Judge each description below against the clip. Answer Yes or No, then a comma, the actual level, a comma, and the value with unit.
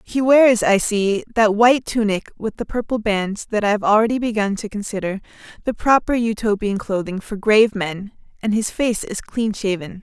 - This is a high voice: Yes, high, 215 Hz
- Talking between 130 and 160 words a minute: No, average, 185 wpm